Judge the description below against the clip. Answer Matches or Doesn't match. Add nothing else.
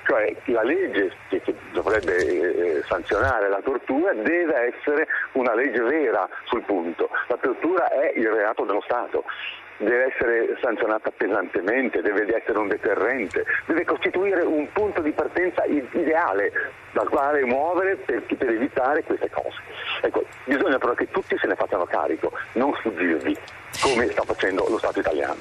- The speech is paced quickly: Doesn't match